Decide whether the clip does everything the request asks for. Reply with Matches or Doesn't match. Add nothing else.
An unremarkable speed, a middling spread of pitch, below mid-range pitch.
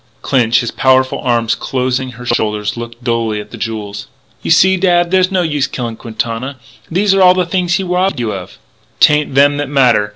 Doesn't match